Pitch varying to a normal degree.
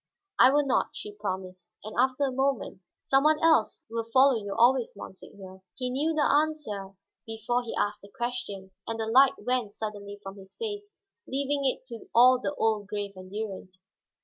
Yes: average, 4.8 semitones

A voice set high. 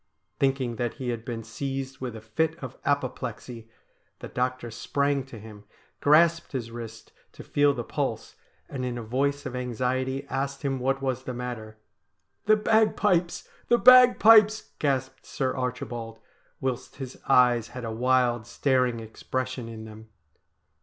No: low, 130 Hz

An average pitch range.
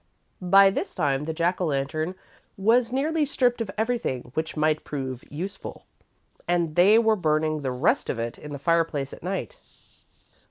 No: wide, 6.0 semitones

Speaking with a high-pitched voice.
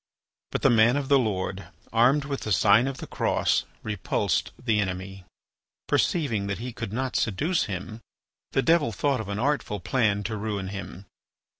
No: low, 110 Hz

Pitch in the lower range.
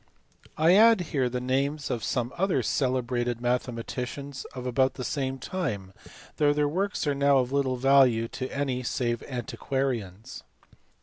Yes: low, 130 Hz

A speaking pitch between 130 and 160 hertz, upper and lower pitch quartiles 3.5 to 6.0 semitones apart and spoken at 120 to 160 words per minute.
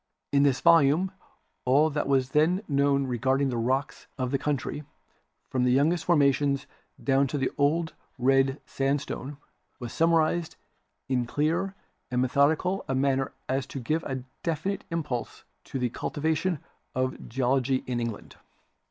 No: medium, 140 Hz; average, 3.1 semitones; average, 150 wpm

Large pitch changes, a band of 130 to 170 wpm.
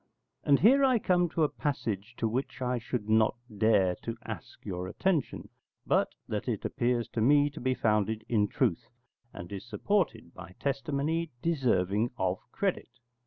Yes: wide, 5.7 semitones; average, 165 wpm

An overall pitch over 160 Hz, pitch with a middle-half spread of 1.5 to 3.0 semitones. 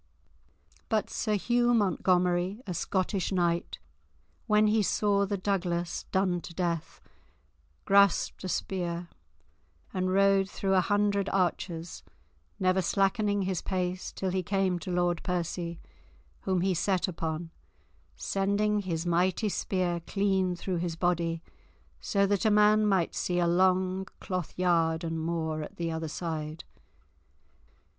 Yes: medium, 185 Hz; narrow, 2.4 semitones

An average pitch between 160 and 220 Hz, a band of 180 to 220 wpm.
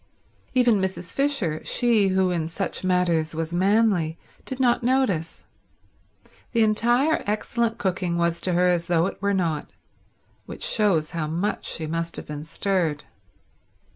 No: medium, 185 Hz; average, 145 wpm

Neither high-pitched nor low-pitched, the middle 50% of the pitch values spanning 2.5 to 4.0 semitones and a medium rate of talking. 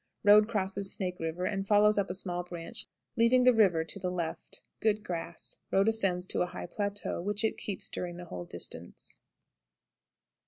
No: high, 195 Hz; average, 3.0 semitones; average, 180 wpm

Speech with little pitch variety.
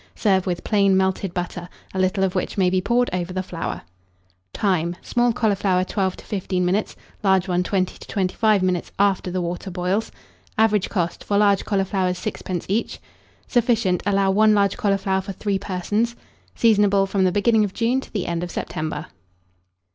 Yes: narrow, 2.2 semitones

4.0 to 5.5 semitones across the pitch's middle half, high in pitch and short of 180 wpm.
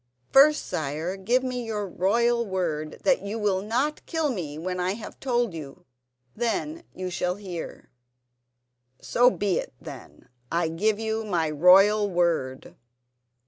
Yes: average, 5.2 semitones; high, 200 Hz; average, 145 wpm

